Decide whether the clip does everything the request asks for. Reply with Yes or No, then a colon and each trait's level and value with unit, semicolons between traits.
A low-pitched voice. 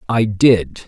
Yes: low, 100 Hz